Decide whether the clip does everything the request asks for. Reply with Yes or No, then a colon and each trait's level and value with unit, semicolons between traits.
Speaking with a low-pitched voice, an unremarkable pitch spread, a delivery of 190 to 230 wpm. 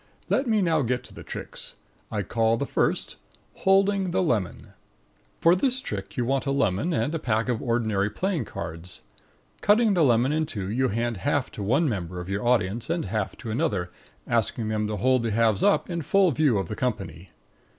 No: low, 120 Hz; wide, 7.2 semitones; average, 200 wpm